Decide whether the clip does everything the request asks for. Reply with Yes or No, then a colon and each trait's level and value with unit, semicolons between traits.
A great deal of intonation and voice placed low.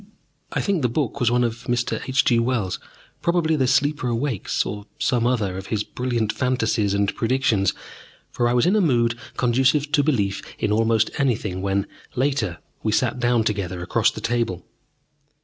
No: average, 3.6 semitones; low, 120 Hz